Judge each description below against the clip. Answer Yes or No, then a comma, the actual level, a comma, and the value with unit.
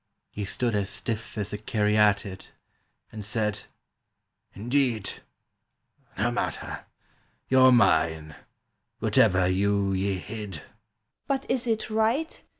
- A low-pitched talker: Yes, low, 105 Hz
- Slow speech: Yes, slow, 110 wpm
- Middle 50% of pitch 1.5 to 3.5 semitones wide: No, average, 3.9 semitones